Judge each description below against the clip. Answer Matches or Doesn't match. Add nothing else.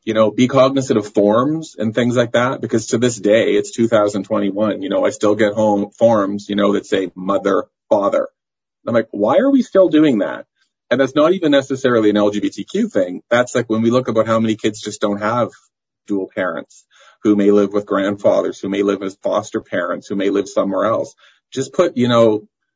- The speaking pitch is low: Matches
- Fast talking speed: Matches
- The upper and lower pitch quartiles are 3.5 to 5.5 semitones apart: Matches